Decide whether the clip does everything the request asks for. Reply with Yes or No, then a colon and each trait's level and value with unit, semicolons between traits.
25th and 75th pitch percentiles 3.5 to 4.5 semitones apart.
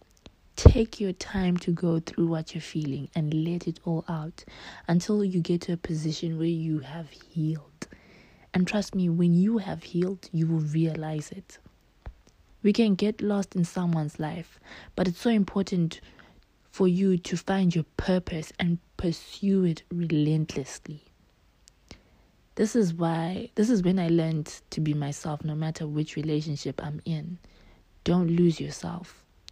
No: average, 2.7 semitones